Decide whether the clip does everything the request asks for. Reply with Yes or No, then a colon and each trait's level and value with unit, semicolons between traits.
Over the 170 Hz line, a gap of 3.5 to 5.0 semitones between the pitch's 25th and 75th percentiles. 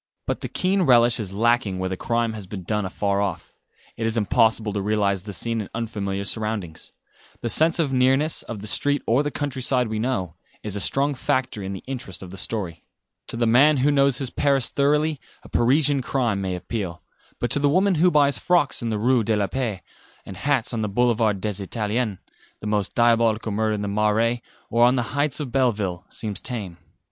No: low, 115 Hz; average, 4.4 semitones